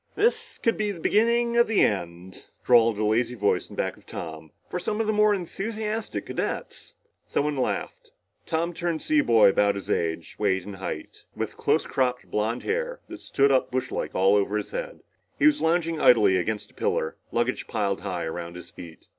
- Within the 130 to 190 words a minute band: No, average, 200 wpm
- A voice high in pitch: No, low, 125 Hz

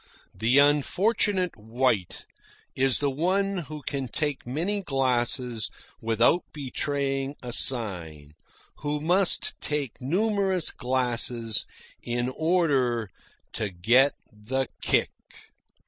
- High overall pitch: No, low, 135 Hz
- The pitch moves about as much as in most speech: Yes, average, 4.4 semitones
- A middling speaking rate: No, slow, 100 wpm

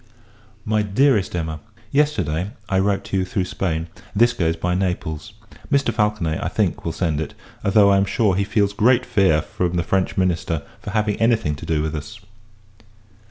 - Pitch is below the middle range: Yes, very low, 95 Hz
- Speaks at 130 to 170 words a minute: No, average, 190 wpm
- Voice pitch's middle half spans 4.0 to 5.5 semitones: Yes, average, 4.3 semitones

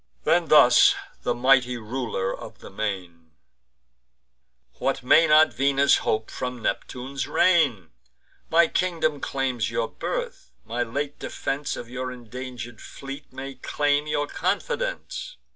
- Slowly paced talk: Yes, slow, 125 wpm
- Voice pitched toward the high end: No, low, 130 Hz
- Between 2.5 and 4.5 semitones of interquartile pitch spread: Yes, average, 3.3 semitones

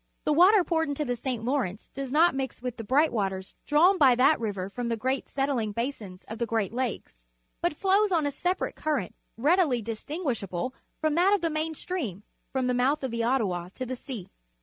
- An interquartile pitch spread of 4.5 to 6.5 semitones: Yes, wide, 5.4 semitones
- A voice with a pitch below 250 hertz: No, very high, 260 Hz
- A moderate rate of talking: No, fast, 215 wpm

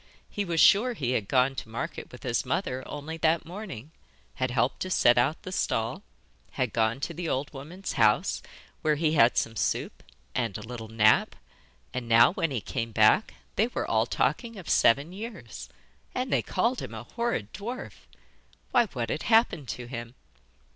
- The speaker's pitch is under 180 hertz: Yes, medium, 140 Hz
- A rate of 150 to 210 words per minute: Yes, average, 180 wpm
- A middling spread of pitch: No, wide, 8.2 semitones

